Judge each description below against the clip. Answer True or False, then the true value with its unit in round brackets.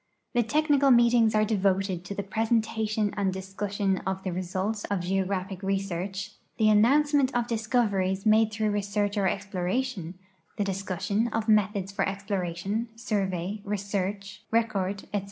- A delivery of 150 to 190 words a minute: False (140 wpm)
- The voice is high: True (205 Hz)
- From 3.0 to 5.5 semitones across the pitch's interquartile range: False (2.4 semitones)